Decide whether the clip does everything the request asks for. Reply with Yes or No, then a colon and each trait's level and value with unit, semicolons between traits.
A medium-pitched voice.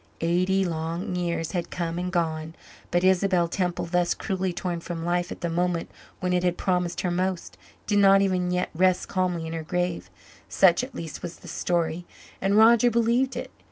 Yes: medium, 180 Hz